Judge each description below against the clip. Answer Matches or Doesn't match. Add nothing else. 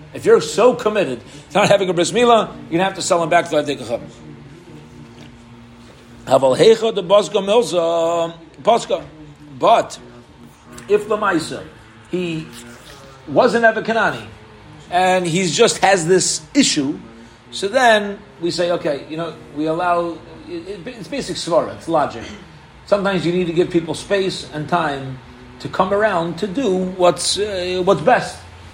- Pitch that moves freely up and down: Matches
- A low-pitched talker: Doesn't match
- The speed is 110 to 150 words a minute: Matches